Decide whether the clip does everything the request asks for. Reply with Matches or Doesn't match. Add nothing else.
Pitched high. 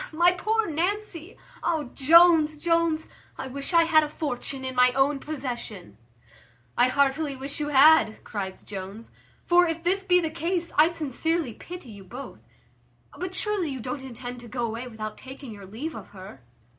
Matches